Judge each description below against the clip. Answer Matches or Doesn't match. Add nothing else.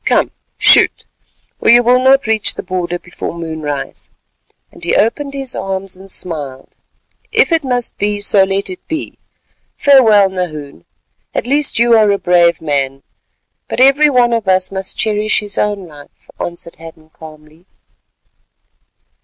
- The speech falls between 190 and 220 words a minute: Doesn't match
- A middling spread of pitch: Doesn't match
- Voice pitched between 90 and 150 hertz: Doesn't match